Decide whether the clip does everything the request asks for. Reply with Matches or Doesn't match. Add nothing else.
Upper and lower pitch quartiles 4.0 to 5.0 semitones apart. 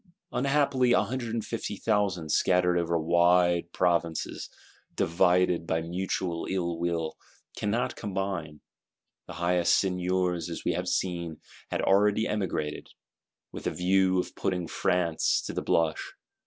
Doesn't match